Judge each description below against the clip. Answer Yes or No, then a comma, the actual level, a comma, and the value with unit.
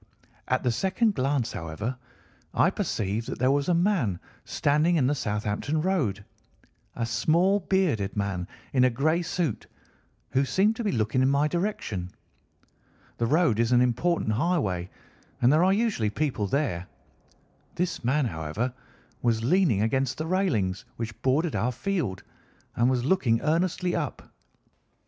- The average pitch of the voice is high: No, low, 130 Hz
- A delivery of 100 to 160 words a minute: Yes, average, 150 wpm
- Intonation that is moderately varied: No, wide, 7.4 semitones